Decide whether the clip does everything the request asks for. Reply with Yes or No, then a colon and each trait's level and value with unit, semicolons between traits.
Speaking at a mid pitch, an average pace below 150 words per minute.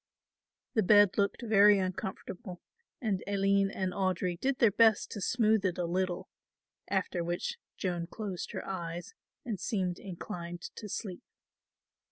No: high, 195 Hz; average, 140 wpm